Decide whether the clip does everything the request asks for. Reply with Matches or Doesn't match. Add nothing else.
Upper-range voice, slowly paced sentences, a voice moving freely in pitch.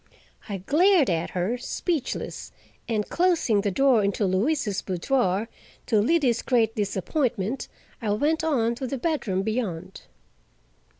Matches